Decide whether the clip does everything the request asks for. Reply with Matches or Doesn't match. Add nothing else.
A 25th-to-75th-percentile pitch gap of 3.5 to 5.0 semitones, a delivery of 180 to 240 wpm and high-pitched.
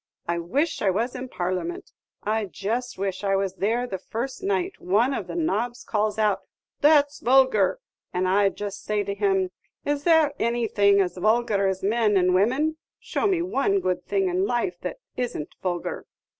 Matches